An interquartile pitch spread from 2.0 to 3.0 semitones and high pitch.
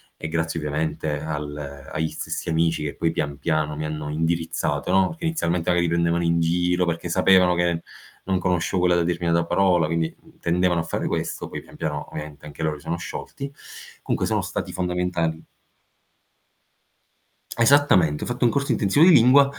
No: narrow, 2.4 semitones; very low, 85 Hz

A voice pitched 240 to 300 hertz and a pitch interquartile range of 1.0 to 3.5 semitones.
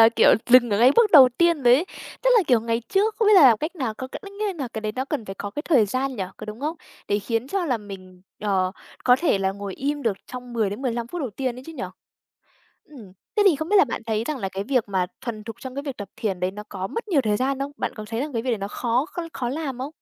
No: high, 245 Hz; wide, 5.4 semitones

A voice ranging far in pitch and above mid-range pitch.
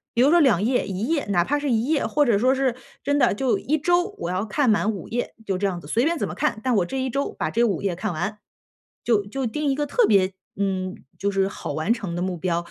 Yes: wide, 6.1 semitones; high, 225 Hz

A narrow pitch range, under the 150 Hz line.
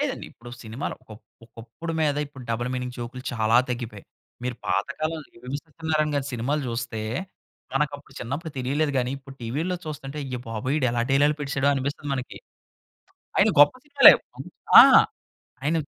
No: average, 3.6 semitones; low, 135 Hz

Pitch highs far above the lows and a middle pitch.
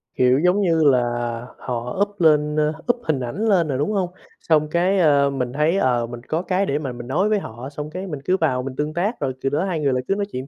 Yes: wide, 5.8 semitones; medium, 150 Hz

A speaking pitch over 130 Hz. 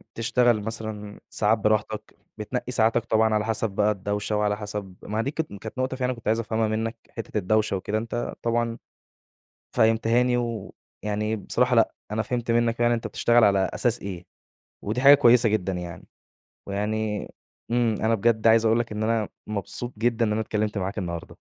No: low, 110 Hz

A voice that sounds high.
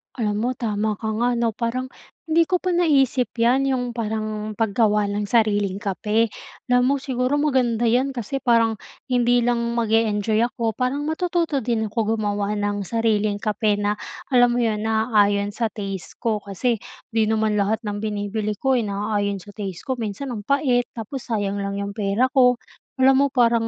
Yes: high, 225 Hz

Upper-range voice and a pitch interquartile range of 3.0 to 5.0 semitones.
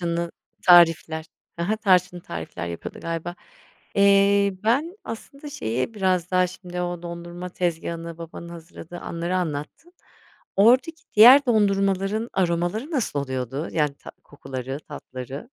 No: medium, 175 Hz; average, 3.4 semitones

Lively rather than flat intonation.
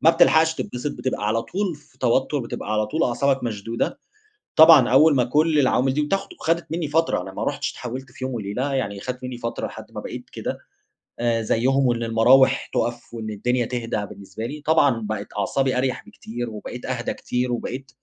No: average, 3.6 semitones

